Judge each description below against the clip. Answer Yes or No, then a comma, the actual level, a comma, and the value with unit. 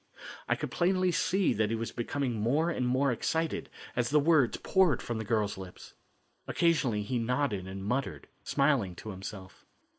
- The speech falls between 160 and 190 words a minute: Yes, average, 170 wpm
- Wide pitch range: Yes, wide, 6.1 semitones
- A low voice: Yes, low, 125 Hz